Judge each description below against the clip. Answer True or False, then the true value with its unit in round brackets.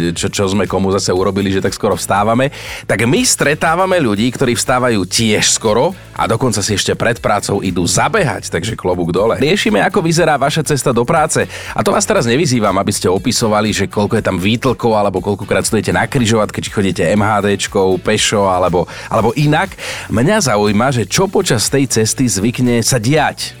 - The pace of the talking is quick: True (180 wpm)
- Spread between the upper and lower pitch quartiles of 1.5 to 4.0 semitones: False (4.7 semitones)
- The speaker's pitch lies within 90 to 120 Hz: True (110 Hz)